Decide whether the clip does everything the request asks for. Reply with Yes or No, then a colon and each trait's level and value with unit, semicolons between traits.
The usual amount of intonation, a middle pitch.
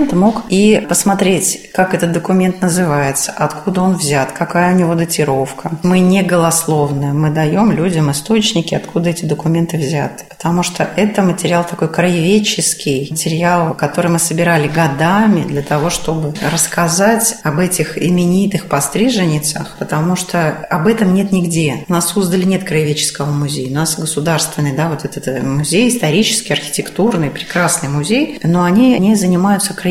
Yes: average, 3.5 semitones; medium, 170 Hz